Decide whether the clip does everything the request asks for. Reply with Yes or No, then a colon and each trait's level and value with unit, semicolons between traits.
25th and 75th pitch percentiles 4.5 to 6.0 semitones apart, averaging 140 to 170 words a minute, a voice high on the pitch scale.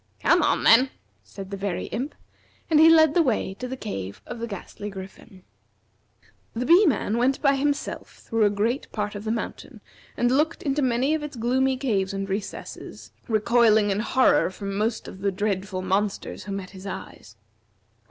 No: average, 4.9 semitones; average, 180 wpm; high, 225 Hz